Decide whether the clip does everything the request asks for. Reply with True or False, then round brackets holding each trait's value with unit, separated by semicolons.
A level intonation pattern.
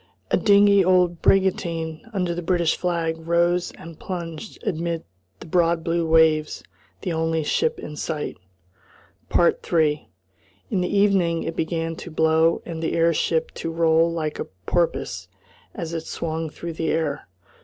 True (1.4 semitones)